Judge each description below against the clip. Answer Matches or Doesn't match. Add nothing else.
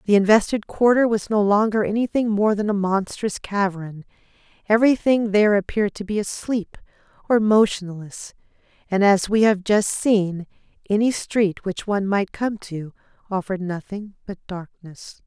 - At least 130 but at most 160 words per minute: Matches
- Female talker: Matches